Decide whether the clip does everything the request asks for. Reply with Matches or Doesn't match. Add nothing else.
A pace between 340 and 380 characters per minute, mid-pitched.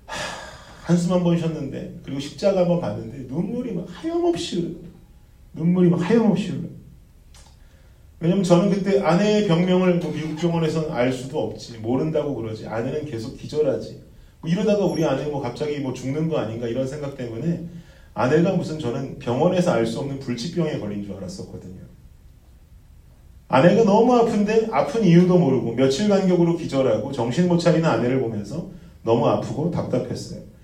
Matches